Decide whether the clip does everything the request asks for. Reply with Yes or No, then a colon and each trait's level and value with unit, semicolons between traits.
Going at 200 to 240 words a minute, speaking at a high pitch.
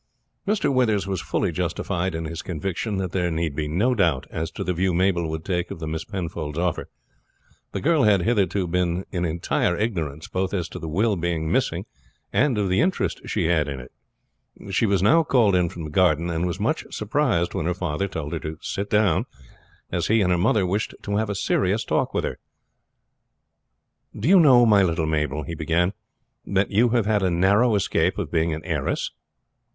No: fast, 205 wpm; very low, 90 Hz